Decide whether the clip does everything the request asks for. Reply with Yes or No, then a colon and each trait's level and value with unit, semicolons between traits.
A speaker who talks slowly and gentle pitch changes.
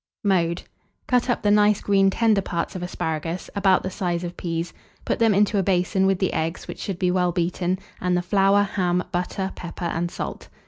No: average, 200 wpm; narrow, 2.2 semitones